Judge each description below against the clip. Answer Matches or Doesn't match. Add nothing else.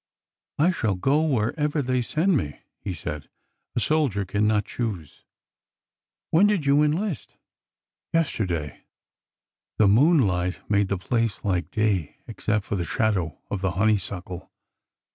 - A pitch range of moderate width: Doesn't match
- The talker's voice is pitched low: Matches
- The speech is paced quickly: Doesn't match